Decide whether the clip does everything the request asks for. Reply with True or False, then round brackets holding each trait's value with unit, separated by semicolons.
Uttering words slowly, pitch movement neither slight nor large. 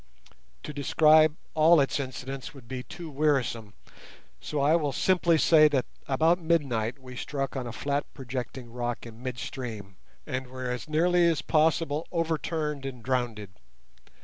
False (150 wpm; 3.9 semitones)